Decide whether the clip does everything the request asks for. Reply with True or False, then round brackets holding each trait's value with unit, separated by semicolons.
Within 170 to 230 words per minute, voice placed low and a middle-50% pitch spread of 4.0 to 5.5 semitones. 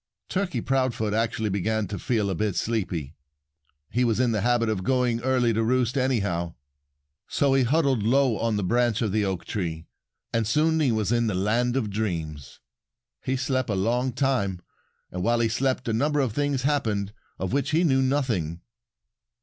True (180 wpm; 115 Hz; 4.3 semitones)